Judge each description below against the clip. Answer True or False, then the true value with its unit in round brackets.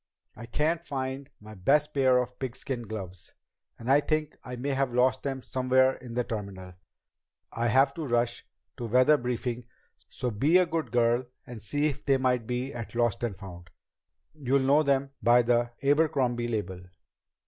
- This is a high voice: False (125 Hz)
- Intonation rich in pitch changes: False (2.7 semitones)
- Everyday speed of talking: True (170 wpm)